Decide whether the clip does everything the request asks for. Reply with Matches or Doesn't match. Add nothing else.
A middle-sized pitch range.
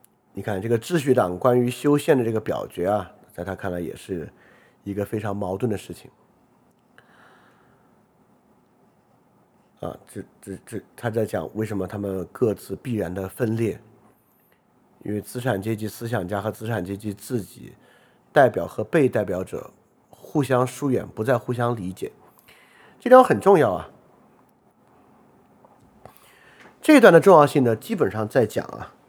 Matches